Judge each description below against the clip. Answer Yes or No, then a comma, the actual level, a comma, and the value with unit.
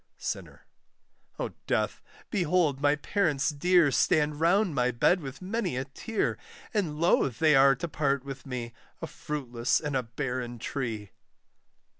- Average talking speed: Yes, average, 145 wpm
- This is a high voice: No, medium, 145 Hz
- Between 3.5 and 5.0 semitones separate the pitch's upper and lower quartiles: Yes, average, 4.6 semitones